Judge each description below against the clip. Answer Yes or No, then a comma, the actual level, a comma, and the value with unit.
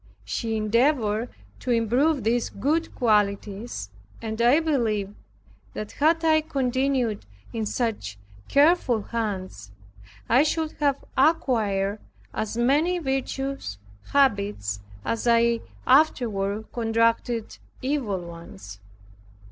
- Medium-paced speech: No, slow, 100 wpm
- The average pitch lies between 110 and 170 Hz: No, high, 235 Hz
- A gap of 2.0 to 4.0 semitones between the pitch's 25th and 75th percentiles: No, average, 4.8 semitones